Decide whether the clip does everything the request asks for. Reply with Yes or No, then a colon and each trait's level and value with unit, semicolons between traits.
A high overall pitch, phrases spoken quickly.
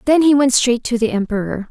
Yes: high, 245 Hz; fast, 245 wpm